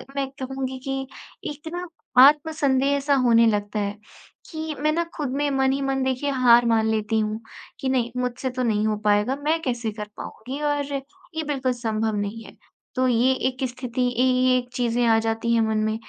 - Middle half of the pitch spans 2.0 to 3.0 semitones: No, average, 3.4 semitones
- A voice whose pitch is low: No, very high, 255 Hz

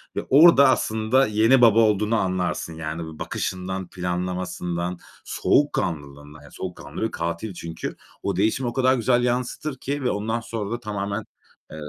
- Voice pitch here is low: Yes, low, 105 Hz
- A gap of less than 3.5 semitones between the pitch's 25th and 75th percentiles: No, average, 5.1 semitones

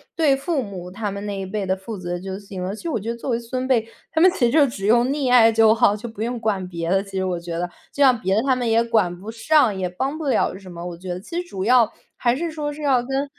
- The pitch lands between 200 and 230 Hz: Yes, high, 225 Hz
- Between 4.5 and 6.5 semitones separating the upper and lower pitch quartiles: Yes, average, 5.2 semitones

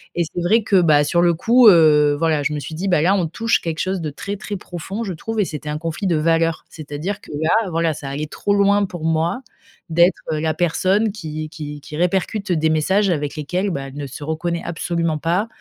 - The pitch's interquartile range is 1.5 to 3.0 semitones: No, average, 3.7 semitones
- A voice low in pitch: No, medium, 165 Hz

